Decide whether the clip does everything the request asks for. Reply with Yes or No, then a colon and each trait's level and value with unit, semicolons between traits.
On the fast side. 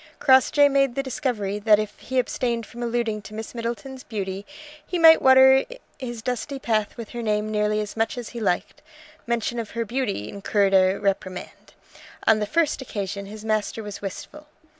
No: average, 180 wpm